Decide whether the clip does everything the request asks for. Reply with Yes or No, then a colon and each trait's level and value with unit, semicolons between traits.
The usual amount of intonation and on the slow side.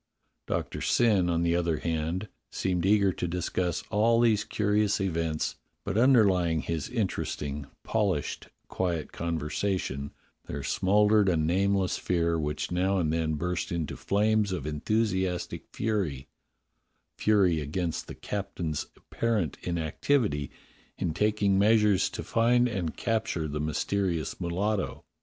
Yes: average, 4.3 semitones; slow, 125 wpm